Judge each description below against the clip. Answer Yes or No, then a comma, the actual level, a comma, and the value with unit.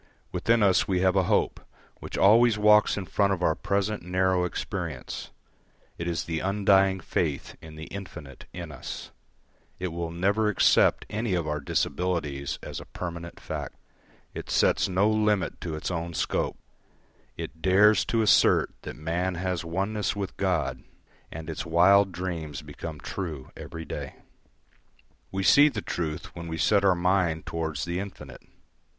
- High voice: No, very low, 90 Hz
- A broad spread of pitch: No, average, 3.2 semitones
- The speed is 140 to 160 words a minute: Yes, average, 155 wpm